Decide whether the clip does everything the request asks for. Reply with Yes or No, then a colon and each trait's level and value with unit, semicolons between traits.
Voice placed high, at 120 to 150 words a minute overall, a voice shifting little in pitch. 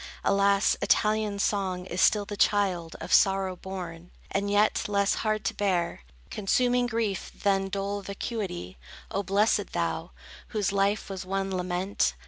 Yes: high, 195 Hz; average, 140 wpm; narrow, 1.7 semitones